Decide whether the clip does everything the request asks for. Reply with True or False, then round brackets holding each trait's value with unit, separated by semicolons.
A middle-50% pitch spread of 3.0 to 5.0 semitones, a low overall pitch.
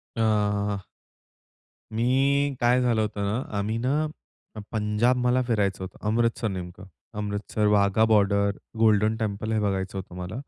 False (2.4 semitones; 105 Hz)